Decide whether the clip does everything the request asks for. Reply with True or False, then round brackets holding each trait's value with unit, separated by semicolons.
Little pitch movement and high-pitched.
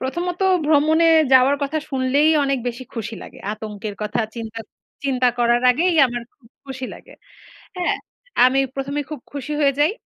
False (3.5 semitones; 265 Hz)